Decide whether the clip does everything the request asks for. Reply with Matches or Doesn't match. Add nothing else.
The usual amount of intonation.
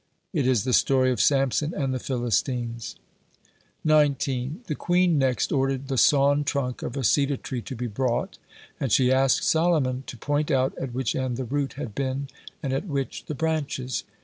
Doesn't match